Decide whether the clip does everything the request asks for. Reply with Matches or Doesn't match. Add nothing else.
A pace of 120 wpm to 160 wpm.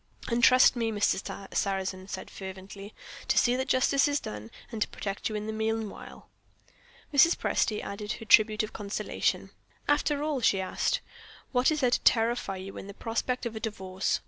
Doesn't match